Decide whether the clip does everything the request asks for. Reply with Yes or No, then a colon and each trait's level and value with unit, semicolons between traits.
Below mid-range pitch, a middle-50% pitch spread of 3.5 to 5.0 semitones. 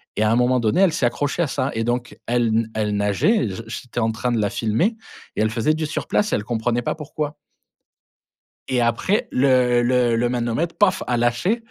Yes: low, 120 Hz; average, 4.1 semitones